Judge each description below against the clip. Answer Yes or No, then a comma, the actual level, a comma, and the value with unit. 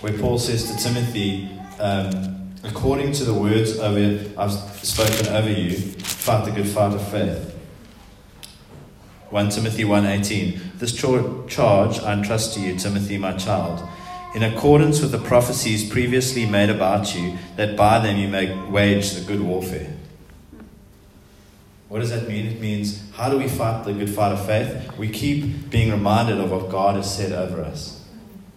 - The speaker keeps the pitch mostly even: Yes, narrow, 2.3 semitones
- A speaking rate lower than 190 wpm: Yes, average, 160 wpm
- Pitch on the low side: Yes, low, 105 Hz